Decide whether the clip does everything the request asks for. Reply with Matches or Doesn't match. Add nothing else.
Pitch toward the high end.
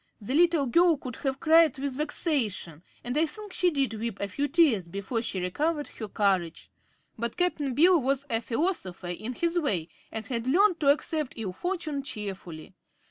Matches